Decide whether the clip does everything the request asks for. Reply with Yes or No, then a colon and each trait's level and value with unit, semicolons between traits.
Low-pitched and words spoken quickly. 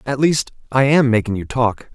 Yes: low, 125 Hz; fast, 215 wpm